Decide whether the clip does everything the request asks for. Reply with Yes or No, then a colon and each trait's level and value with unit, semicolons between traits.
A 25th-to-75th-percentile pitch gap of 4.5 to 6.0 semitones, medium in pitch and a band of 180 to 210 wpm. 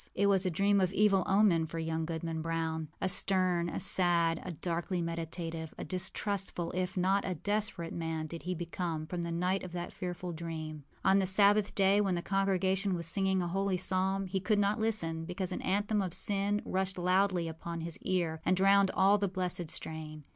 No: average, 2.7 semitones; medium, 180 Hz; average, 195 wpm